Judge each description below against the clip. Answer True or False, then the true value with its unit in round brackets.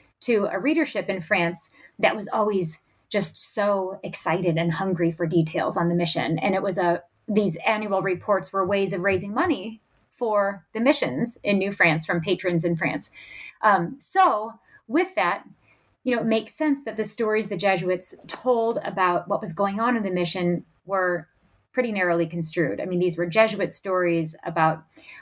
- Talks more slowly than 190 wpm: True (175 wpm)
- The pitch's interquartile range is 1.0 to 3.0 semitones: False (4.3 semitones)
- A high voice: True (195 Hz)